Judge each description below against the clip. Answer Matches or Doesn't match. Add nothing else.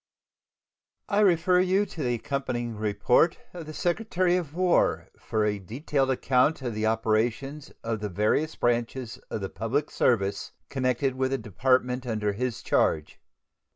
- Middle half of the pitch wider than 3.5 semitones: Matches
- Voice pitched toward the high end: Doesn't match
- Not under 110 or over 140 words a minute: Doesn't match